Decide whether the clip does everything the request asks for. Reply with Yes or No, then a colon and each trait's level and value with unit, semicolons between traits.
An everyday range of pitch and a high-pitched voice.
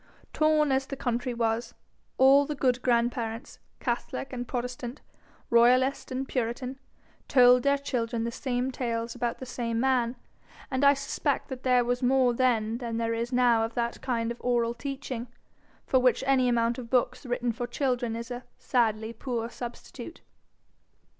No: narrow, 1.8 semitones; high, 245 Hz